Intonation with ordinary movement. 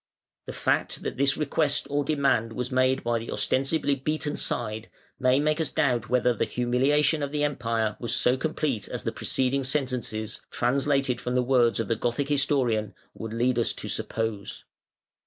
Yes: average, 3.3 semitones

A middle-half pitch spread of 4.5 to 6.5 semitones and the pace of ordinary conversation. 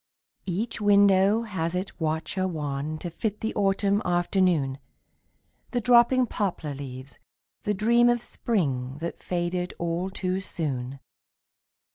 No: average, 4.8 semitones; slow, 120 wpm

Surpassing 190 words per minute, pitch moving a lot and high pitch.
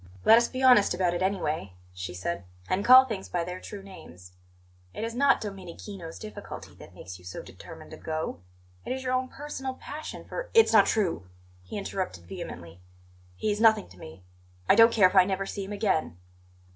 Yes: average, 200 wpm; wide, 6.3 semitones; high, 195 Hz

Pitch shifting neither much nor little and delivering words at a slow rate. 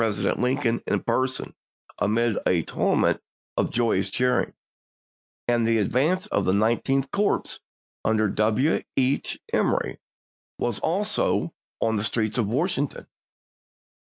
Yes: average, 3.8 semitones; slow, 125 wpm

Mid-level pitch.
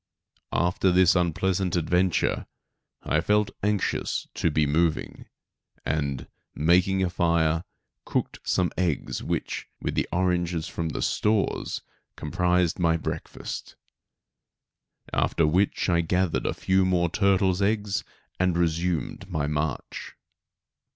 No: very low, 90 Hz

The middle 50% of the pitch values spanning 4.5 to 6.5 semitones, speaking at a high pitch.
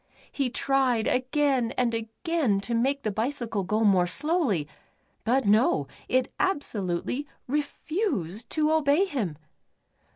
Yes: average, 5.2 semitones; very high, 250 Hz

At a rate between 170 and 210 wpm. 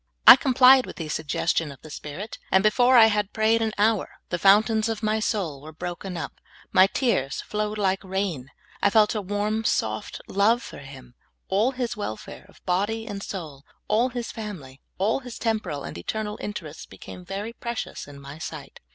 Yes: average, 190 wpm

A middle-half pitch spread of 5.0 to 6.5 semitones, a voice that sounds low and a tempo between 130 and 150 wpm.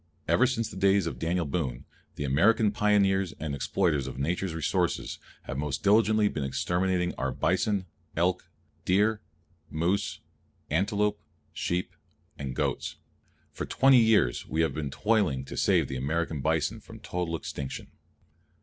Yes: wide, 5.6 semitones; very low, 90 Hz; average, 140 wpm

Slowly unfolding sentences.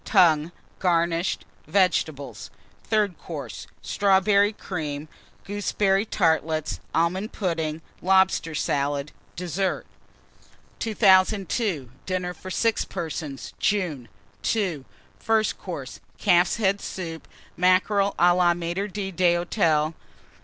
Yes: slow, 90 wpm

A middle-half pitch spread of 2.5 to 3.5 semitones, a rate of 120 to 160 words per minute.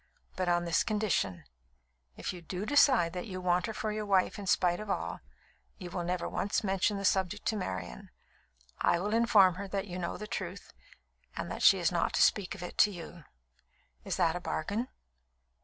No: average, 3.0 semitones; average, 200 wpm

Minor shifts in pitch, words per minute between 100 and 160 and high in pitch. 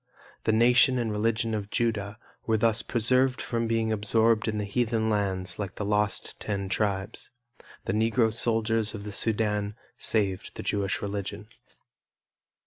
No: narrow, 1.9 semitones; average, 140 wpm; low, 110 Hz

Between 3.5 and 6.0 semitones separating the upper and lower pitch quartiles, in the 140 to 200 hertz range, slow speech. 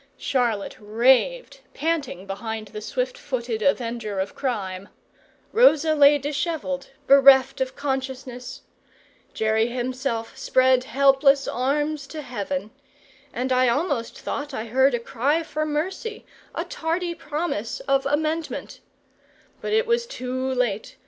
No: average, 3.9 semitones; very high, 265 Hz; slow, 120 wpm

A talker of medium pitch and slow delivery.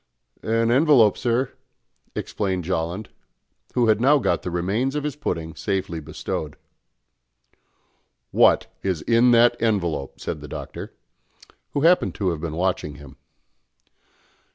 No: low, 100 Hz; slow, 130 wpm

